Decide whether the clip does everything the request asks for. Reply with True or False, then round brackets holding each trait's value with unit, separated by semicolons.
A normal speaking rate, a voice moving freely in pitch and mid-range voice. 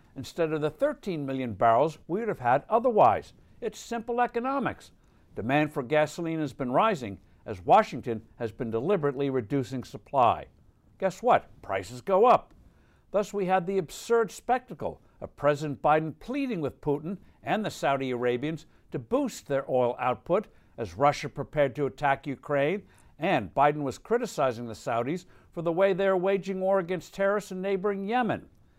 True (160 wpm; 6.5 semitones; 150 Hz)